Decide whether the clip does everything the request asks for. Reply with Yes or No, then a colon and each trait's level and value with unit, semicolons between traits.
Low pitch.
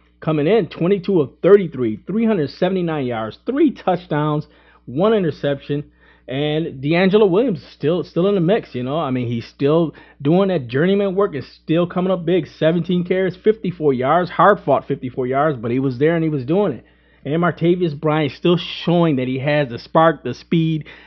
No: medium, 160 Hz